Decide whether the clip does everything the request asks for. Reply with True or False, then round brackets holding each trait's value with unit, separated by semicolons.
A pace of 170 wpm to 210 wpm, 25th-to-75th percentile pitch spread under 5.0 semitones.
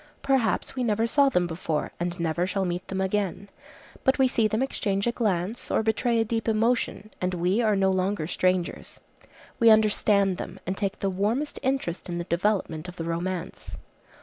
True (185 wpm; 4.0 semitones)